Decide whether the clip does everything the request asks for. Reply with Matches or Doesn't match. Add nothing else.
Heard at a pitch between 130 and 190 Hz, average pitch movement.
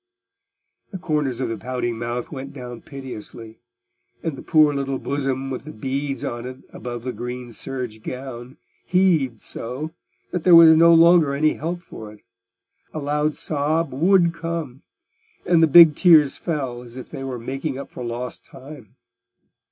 Matches